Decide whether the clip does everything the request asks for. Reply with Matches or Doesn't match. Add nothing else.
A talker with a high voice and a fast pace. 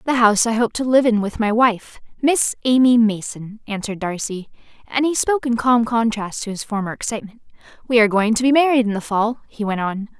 Matches